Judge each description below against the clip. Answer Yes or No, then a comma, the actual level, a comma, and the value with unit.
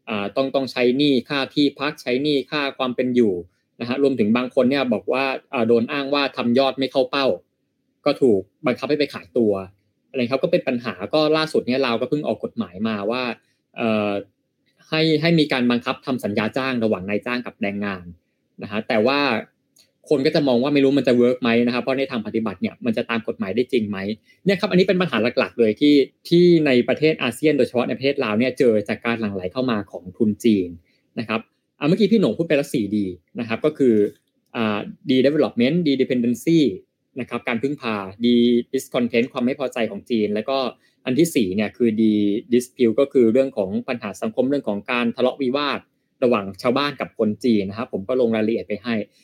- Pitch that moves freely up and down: No, average, 3.8 semitones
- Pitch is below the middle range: Yes, low, 125 Hz